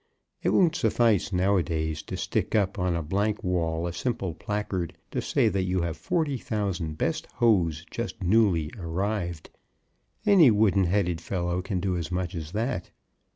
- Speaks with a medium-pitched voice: No, very low, 95 Hz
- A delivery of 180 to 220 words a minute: No, average, 170 wpm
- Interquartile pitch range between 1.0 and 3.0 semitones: No, average, 3.8 semitones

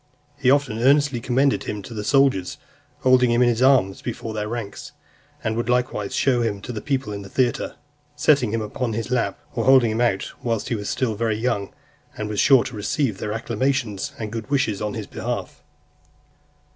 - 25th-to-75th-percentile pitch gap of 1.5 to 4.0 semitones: Yes, average, 3.3 semitones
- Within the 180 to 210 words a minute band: Yes, average, 195 wpm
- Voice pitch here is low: Yes, low, 115 Hz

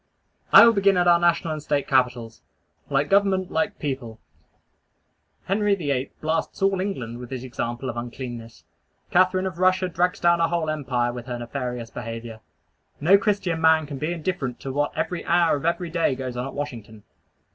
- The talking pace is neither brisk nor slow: Yes, average, 180 wpm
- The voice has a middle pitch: Yes, medium, 150 Hz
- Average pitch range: No, wide, 6.4 semitones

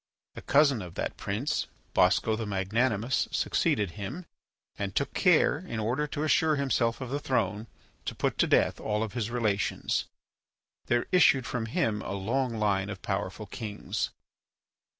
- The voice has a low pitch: Yes, low, 115 Hz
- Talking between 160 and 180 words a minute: No, average, 150 wpm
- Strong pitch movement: No, average, 4.6 semitones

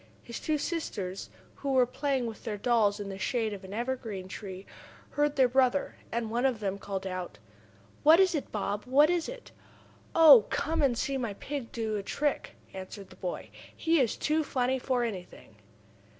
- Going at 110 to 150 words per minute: No, average, 185 wpm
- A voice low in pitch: No, high, 240 Hz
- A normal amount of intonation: No, wide, 5.7 semitones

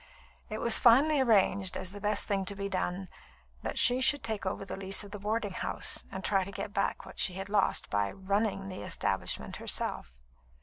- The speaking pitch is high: Yes, high, 200 Hz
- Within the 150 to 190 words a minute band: No, fast, 205 wpm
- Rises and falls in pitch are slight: Yes, narrow, 2.1 semitones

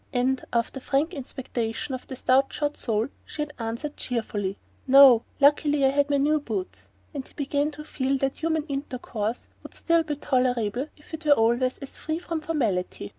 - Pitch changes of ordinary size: Yes, average, 3.6 semitones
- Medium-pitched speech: No, very high, 270 Hz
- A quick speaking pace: No, average, 180 wpm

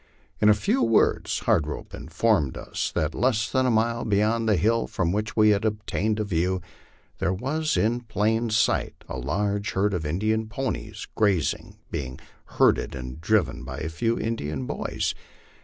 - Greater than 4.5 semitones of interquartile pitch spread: Yes, average, 4.9 semitones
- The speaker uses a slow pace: No, average, 170 wpm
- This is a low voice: Yes, low, 105 Hz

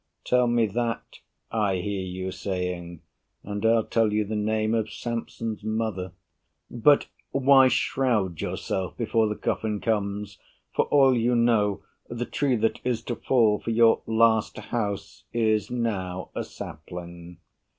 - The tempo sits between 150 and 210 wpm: No, average, 140 wpm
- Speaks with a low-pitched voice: Yes, low, 110 Hz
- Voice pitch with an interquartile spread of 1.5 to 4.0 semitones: Yes, average, 2.9 semitones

